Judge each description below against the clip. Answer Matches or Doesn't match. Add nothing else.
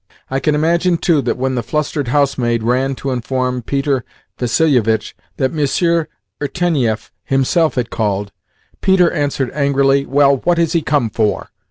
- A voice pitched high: Doesn't match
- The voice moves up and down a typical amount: Matches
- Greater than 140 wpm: Matches